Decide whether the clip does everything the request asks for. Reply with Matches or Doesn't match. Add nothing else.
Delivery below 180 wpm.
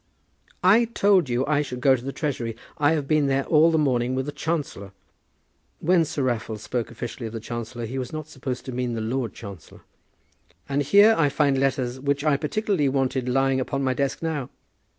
Doesn't match